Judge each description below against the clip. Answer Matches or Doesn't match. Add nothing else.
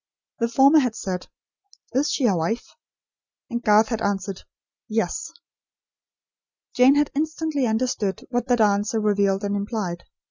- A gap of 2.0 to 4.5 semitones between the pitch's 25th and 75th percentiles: Matches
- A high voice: Matches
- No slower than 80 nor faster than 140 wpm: Matches